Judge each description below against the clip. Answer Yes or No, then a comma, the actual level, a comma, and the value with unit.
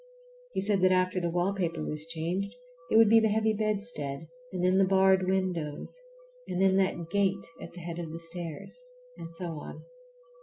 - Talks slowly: No, average, 185 wpm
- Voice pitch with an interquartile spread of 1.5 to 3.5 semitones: Yes, average, 2.8 semitones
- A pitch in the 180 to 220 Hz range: Yes, medium, 185 Hz